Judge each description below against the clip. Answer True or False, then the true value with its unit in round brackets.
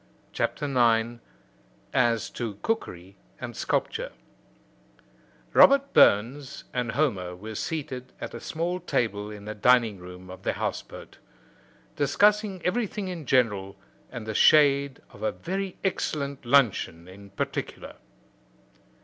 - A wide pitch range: True (8.1 semitones)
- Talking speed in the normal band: False (125 wpm)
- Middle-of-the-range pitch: False (125 Hz)